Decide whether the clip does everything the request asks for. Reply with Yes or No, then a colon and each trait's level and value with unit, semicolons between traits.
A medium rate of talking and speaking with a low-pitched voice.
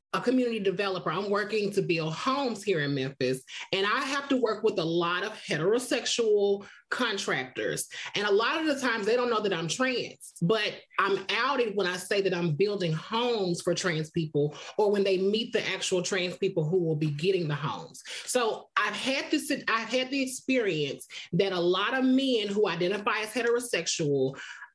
No: average, 190 wpm; high, 200 Hz